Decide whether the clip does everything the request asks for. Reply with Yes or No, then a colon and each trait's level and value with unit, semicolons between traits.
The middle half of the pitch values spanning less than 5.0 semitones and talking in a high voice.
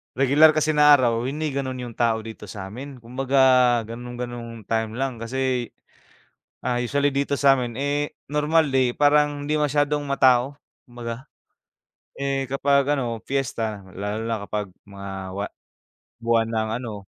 No: average, 3.6 semitones; low, 130 Hz